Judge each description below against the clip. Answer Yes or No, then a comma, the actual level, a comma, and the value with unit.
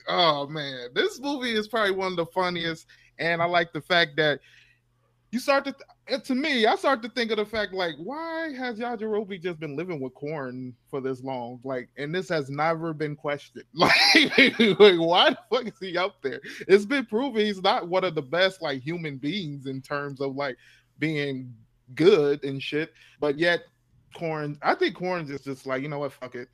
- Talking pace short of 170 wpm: No, fast, 205 wpm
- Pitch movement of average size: No, wide, 7.0 semitones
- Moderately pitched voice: Yes, medium, 165 Hz